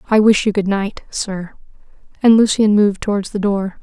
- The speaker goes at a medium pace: Yes, average, 190 wpm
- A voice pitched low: No, high, 205 Hz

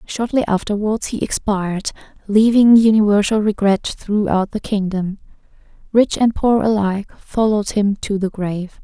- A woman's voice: Yes, female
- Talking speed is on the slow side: Yes, slow, 130 wpm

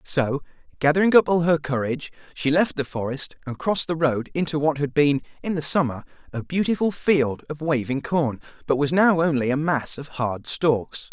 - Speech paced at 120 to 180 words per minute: No, average, 195 wpm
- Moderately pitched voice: Yes, medium, 150 Hz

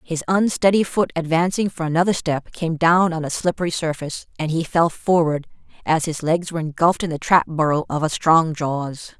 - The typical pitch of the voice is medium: Yes, medium, 165 Hz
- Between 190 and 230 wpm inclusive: Yes, average, 195 wpm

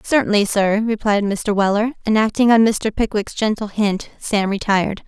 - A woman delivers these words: Yes, female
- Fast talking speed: No, average, 165 wpm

